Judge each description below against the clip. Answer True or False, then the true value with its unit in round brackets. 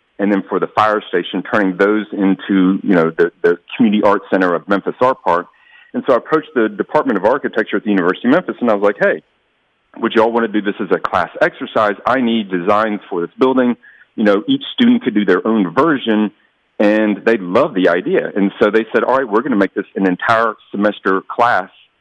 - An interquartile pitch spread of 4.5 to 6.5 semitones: True (4.8 semitones)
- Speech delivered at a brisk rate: True (230 wpm)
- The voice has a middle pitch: False (110 Hz)